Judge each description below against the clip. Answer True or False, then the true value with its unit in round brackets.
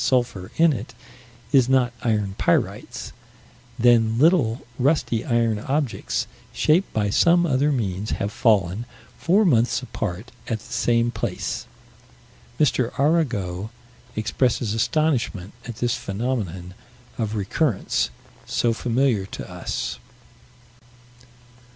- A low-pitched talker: True (120 Hz)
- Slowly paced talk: True (110 wpm)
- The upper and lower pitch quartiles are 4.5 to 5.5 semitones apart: False (4.1 semitones)